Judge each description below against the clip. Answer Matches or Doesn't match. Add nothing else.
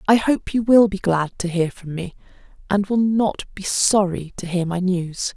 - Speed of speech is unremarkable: Doesn't match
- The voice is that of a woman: Matches